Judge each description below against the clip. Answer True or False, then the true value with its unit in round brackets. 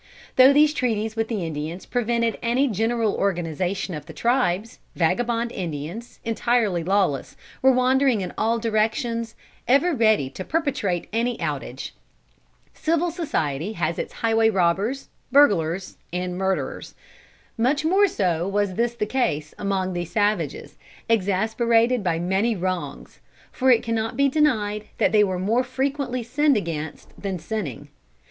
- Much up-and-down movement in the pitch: False (5.0 semitones)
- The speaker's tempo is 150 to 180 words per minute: False (140 wpm)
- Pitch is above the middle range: True (220 Hz)